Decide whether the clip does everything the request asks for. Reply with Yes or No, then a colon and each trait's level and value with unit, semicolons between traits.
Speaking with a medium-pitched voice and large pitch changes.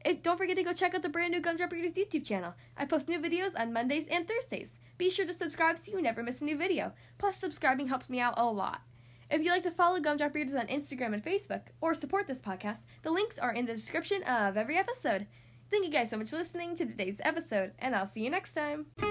No: very high, 315 Hz; wide, 6.5 semitones